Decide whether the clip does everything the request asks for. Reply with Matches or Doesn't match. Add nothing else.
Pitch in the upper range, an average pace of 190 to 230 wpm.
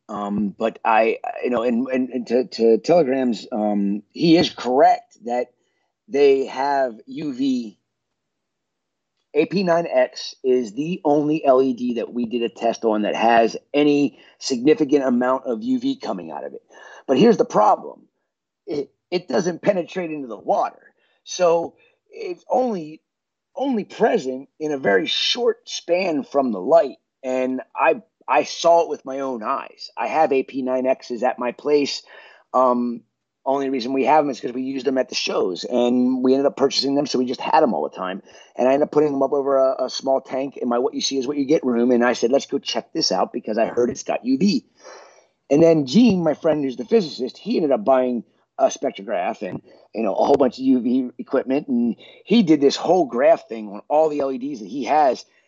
Doesn't match